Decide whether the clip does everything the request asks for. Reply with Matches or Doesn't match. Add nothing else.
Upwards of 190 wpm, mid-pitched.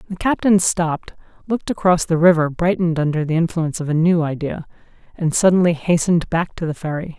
Doesn't match